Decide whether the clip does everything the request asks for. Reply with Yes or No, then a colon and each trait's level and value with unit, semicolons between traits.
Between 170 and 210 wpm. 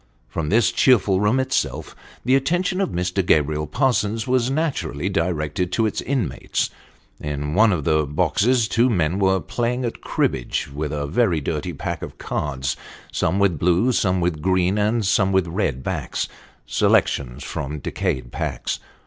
No: average, 155 wpm